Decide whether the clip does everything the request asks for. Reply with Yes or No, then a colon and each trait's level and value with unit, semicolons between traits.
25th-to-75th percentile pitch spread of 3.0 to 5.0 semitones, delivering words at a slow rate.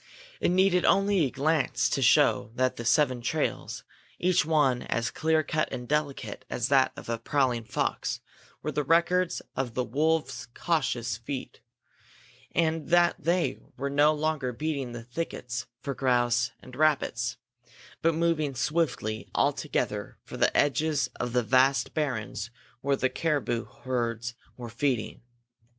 No: average, 4.5 semitones; average, 145 wpm